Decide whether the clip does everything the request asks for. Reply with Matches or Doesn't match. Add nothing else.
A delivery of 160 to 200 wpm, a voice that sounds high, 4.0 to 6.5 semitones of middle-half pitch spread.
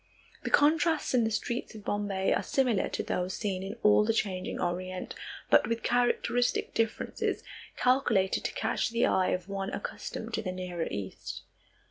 Matches